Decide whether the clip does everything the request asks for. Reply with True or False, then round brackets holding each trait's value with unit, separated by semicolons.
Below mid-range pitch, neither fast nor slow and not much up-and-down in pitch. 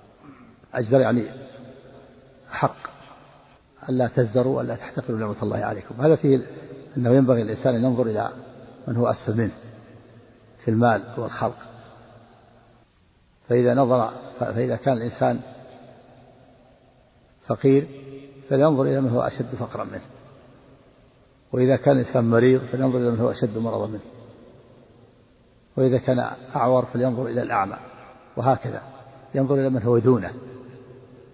True (125 Hz; 115 wpm; 1.9 semitones)